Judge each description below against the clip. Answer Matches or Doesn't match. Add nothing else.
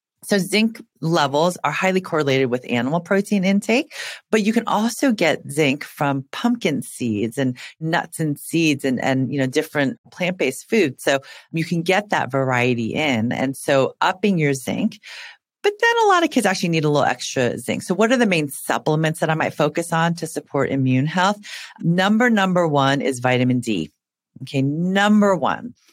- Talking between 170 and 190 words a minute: Matches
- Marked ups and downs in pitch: Matches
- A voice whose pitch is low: Doesn't match